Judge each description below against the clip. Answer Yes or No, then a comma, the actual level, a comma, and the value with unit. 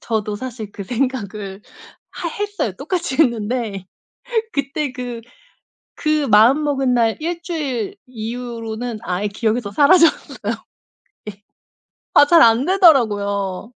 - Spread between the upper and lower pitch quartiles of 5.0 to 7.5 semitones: Yes, average, 5.3 semitones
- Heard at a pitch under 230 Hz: No, high, 245 Hz